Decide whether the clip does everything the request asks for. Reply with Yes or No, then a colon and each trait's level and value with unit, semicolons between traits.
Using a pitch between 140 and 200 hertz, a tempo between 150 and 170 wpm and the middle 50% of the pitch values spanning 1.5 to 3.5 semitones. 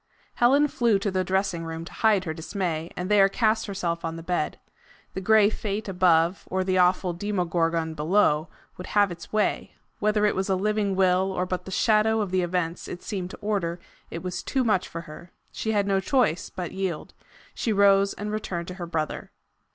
No: high, 190 Hz; fast, 205 wpm; average, 3.2 semitones